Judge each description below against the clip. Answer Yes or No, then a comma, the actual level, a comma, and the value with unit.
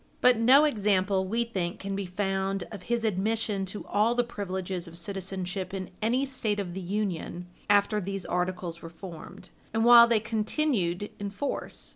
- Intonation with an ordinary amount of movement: Yes, average, 3.2 semitones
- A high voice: Yes, high, 200 Hz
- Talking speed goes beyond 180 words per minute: No, average, 170 wpm